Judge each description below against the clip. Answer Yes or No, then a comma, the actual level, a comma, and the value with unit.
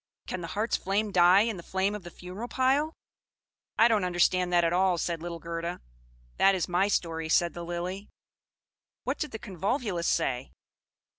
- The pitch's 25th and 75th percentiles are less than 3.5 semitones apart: Yes, average, 3.1 semitones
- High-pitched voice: No, medium, 180 Hz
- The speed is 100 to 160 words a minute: No, average, 175 wpm